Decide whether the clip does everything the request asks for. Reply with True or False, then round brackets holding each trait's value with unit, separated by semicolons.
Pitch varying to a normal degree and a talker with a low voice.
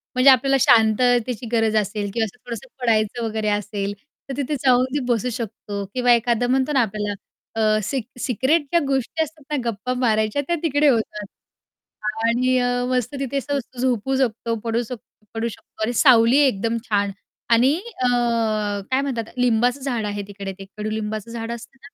False (3.2 semitones; 235 Hz)